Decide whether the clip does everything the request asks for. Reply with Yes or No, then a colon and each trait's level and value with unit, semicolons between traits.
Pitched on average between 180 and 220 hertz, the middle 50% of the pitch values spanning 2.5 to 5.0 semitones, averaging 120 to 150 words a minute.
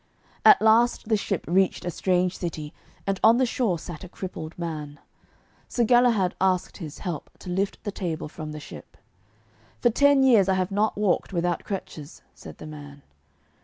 No: medium, 185 Hz; average, 4.7 semitones; average, 175 wpm